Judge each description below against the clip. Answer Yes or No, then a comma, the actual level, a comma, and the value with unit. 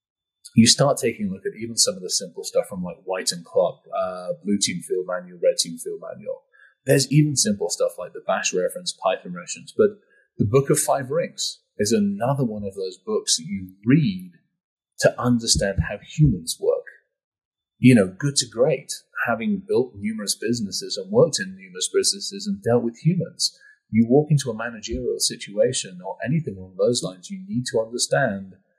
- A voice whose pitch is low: No, medium, 185 Hz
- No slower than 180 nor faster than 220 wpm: Yes, average, 185 wpm